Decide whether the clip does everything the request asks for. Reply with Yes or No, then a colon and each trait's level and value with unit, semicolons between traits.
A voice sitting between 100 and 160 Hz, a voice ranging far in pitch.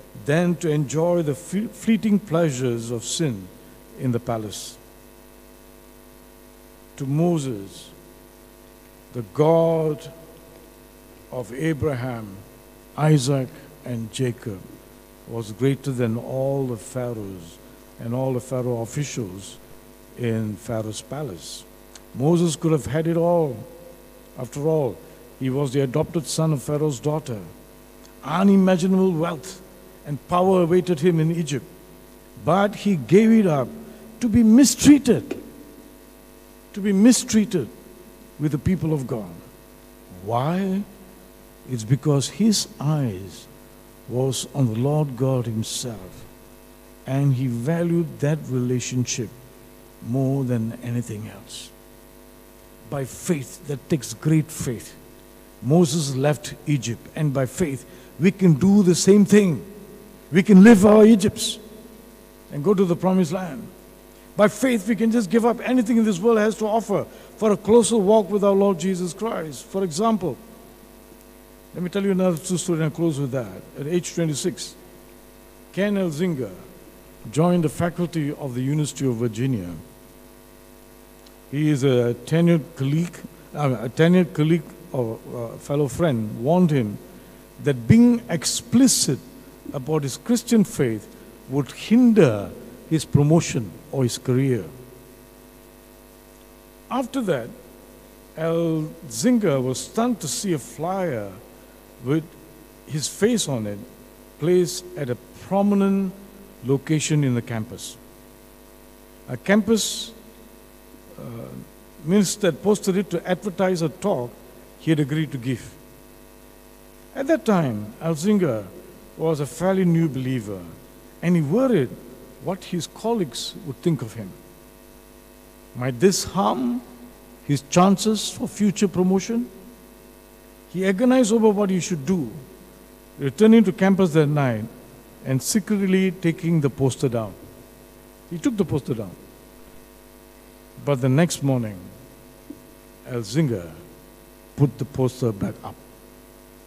Yes: medium, 140 Hz; wide, 7.3 semitones